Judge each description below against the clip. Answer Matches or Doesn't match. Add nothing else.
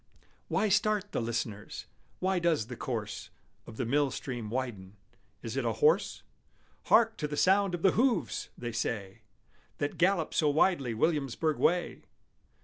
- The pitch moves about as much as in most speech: Doesn't match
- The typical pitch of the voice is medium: Matches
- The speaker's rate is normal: Matches